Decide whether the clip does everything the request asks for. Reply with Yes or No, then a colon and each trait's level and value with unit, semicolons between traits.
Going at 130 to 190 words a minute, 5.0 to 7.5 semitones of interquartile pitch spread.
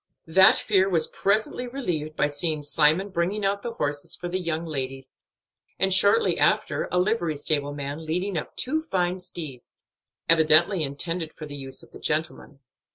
No: average, 165 wpm; average, 4.3 semitones